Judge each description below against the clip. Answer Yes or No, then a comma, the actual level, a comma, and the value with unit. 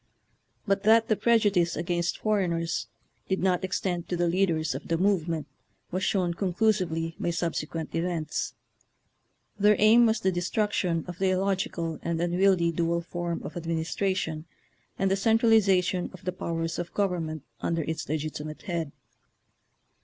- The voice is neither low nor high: Yes, medium, 175 Hz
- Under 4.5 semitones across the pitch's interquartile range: Yes, average, 2.8 semitones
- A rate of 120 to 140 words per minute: No, average, 155 wpm